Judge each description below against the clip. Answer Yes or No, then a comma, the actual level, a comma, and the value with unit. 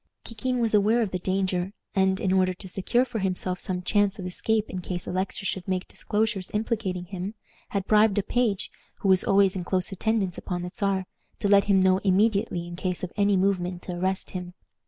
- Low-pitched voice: No, high, 190 Hz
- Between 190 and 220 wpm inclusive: Yes, fast, 205 wpm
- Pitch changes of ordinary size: No, narrow, 2.0 semitones